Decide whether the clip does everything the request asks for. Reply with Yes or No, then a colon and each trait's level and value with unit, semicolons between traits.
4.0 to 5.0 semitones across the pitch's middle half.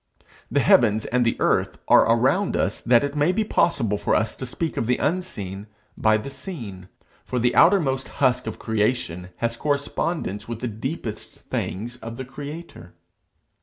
Yes: average, 4.7 semitones